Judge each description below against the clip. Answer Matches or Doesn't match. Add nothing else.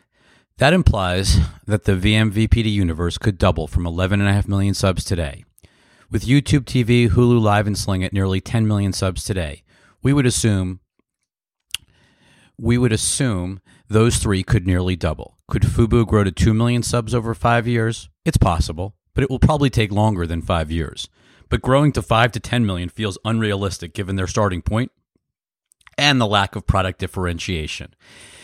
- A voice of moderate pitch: Doesn't match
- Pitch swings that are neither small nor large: Matches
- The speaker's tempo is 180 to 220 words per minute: Doesn't match